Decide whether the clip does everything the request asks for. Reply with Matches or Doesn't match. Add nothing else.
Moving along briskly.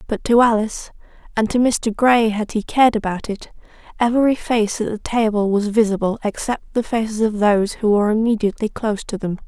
Doesn't match